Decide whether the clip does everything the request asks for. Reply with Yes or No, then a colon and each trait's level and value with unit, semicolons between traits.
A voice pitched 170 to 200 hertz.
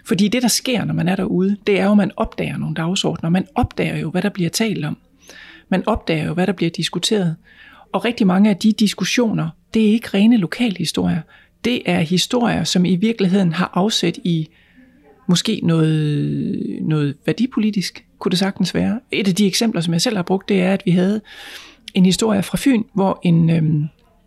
Yes: high, 190 Hz